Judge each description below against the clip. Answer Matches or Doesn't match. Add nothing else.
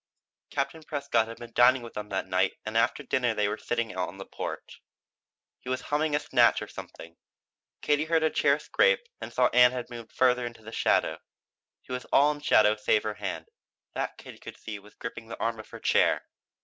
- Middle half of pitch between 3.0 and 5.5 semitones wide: Matches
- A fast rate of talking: Matches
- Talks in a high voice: Doesn't match